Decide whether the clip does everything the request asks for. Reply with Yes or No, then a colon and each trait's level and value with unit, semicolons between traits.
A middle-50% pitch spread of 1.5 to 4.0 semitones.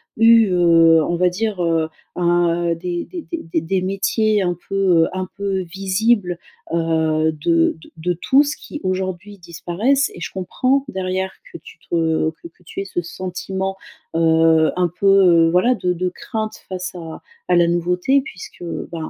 Yes: average, 2.7 semitones